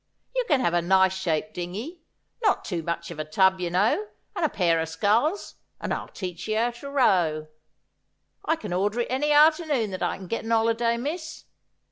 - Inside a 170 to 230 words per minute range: Yes, average, 195 wpm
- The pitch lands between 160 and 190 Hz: No, high, 210 Hz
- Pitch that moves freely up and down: Yes, wide, 7.9 semitones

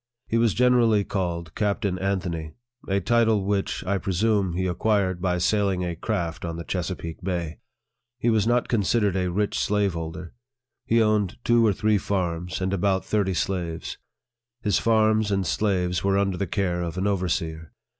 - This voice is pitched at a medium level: No, very low, 95 Hz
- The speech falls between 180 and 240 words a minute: No, average, 165 wpm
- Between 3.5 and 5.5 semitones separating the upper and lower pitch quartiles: No, average, 3.0 semitones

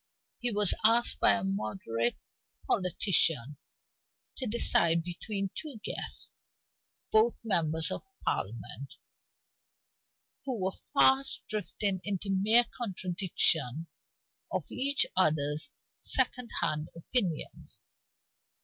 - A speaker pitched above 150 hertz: Yes, high, 190 Hz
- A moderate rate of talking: No, slow, 95 wpm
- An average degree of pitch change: No, wide, 6.6 semitones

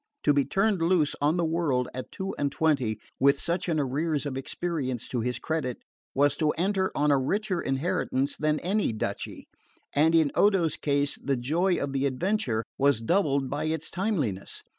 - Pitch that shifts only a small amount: No, average, 4.3 semitones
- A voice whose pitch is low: No, medium, 150 Hz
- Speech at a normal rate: Yes, average, 180 wpm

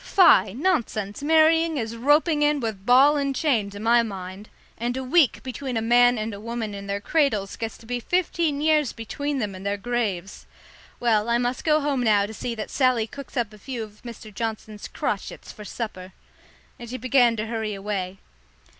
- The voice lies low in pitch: No, high, 235 Hz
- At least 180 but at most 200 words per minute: Yes, average, 195 wpm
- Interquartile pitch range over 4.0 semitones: Yes, average, 4.7 semitones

